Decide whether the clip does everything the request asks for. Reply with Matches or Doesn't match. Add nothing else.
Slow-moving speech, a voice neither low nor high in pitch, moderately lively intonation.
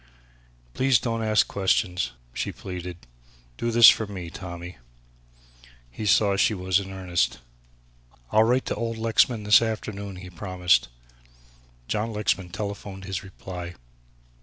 Doesn't match